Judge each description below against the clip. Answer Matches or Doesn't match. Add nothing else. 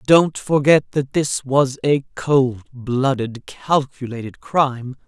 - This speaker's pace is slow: Matches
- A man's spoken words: Doesn't match